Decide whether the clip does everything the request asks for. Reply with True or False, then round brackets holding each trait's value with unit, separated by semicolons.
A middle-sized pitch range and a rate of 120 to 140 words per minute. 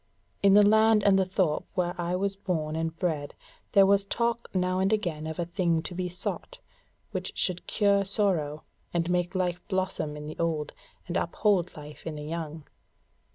False (3.4 semitones; 185 wpm)